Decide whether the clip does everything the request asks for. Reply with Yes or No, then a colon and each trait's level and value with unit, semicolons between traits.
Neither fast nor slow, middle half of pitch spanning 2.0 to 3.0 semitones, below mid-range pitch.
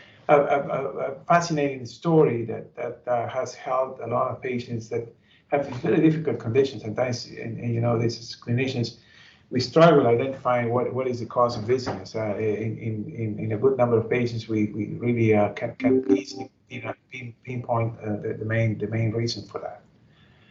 Yes: average, 190 wpm; narrow, 2.6 semitones; low, 120 Hz